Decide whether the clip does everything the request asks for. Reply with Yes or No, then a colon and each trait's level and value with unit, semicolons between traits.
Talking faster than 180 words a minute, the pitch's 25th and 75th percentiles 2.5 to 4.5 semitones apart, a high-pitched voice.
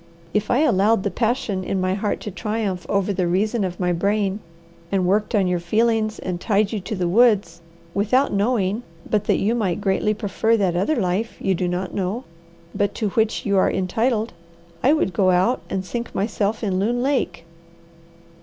Yes: average, 190 wpm; average, 3.1 semitones; high, 200 Hz